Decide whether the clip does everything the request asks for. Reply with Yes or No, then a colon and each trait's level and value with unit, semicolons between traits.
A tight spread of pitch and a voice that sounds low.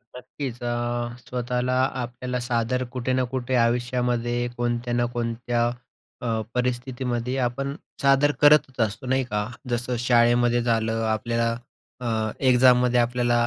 Yes: narrow, 1.0 semitones; low, 120 Hz